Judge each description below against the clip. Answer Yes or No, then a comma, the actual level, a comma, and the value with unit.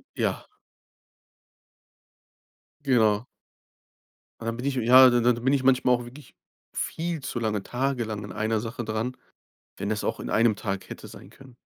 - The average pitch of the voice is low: Yes, low, 120 Hz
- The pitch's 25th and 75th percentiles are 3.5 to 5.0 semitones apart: No, average, 2.9 semitones